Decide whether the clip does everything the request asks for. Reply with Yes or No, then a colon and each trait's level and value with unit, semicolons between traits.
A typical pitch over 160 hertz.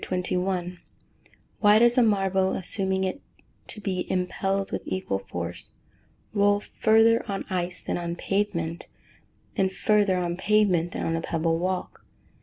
Yes: high, 190 Hz